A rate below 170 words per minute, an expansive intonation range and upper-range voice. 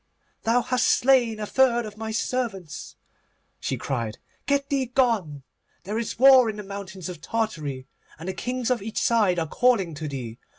No: average, 175 wpm; wide, 5.9 semitones; high, 220 Hz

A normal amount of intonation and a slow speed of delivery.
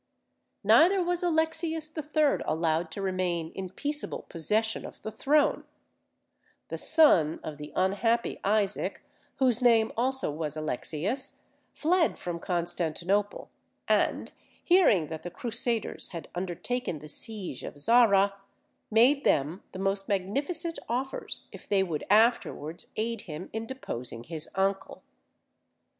No: wide, 7.5 semitones; slow, 125 wpm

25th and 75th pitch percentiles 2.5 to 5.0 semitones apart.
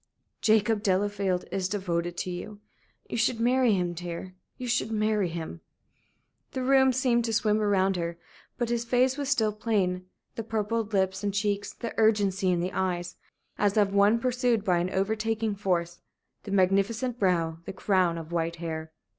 Yes: average, 3.6 semitones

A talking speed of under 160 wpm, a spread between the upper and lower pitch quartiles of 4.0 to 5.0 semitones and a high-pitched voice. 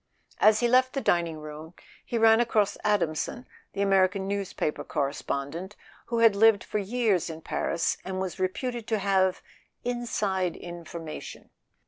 Yes: average, 145 wpm; average, 4.6 semitones; high, 195 Hz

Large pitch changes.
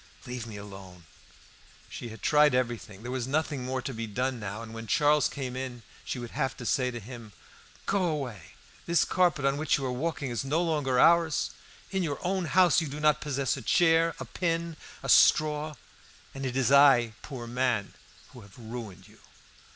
No: average, 4.4 semitones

